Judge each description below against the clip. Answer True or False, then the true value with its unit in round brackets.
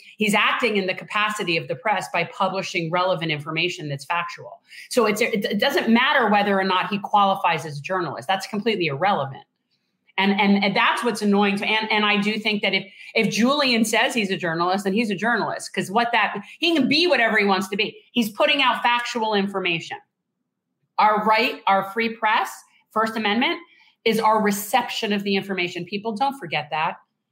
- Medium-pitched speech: False (210 Hz)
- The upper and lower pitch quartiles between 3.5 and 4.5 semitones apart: False (3.1 semitones)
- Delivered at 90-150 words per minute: False (190 wpm)